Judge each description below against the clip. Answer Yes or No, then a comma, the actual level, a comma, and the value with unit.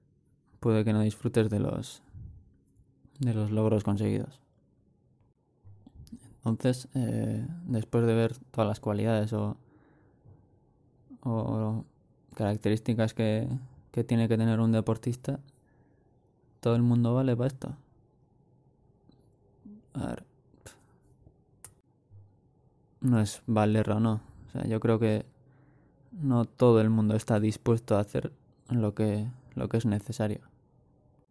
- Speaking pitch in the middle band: No, low, 115 Hz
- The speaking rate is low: Yes, slow, 115 wpm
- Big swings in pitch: No, average, 3.2 semitones